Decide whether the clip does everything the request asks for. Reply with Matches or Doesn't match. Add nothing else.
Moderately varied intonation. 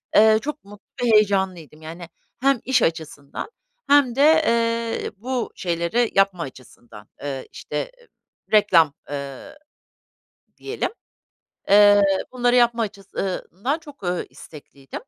Doesn't match